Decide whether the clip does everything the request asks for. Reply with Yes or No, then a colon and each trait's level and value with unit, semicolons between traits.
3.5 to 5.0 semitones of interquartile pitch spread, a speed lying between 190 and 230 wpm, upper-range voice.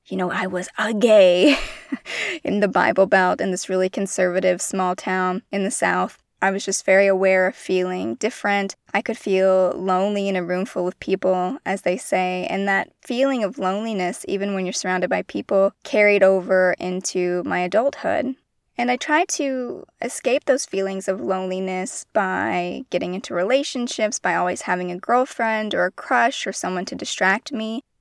No: average, 3.9 semitones; average, 175 wpm; high, 195 Hz